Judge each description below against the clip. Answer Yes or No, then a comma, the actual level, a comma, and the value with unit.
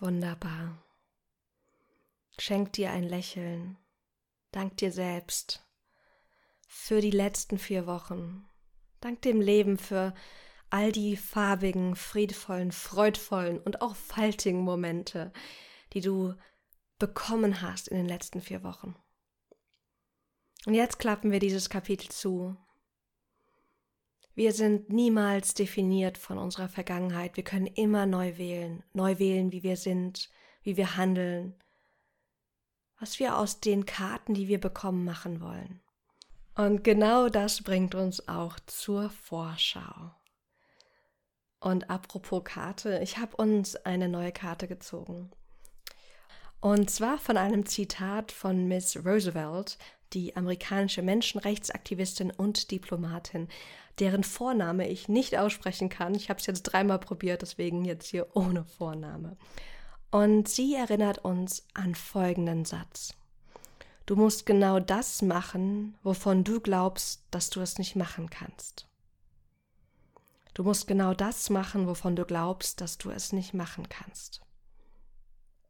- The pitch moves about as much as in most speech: No, narrow, 2.3 semitones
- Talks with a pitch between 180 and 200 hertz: Yes, high, 190 Hz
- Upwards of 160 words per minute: No, slow, 125 wpm